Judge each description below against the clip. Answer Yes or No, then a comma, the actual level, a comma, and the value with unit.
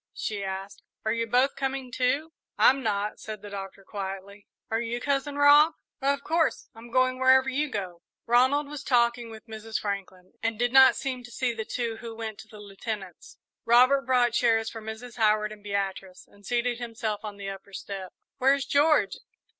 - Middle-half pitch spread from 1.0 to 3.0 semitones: No, average, 4.0 semitones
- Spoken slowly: No, average, 185 wpm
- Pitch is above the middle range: Yes, high, 230 Hz